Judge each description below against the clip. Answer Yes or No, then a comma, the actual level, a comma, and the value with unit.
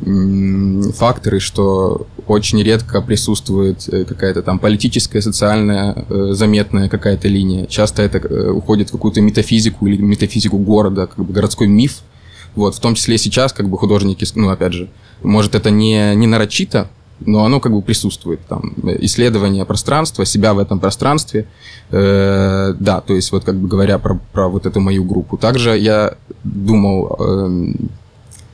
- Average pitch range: No, narrow, 1.8 semitones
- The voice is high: No, low, 105 Hz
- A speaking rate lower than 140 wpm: No, average, 145 wpm